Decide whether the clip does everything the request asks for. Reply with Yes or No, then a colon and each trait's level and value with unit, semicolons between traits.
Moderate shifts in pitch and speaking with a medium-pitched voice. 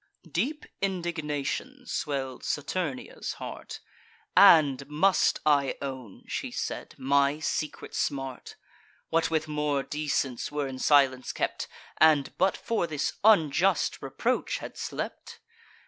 Yes: average, 3.5 semitones; medium, 150 Hz